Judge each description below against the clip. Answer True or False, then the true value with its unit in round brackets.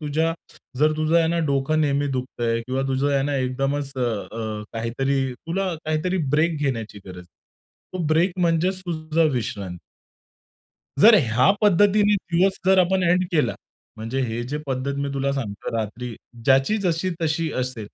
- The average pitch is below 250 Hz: True (140 Hz)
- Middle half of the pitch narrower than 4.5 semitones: False (4.8 semitones)